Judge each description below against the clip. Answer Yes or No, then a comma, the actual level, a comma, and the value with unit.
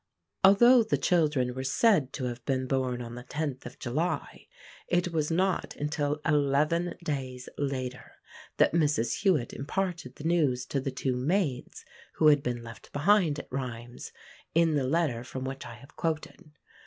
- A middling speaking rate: Yes, average, 165 wpm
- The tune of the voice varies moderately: Yes, average, 4.6 semitones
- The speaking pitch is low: No, medium, 145 Hz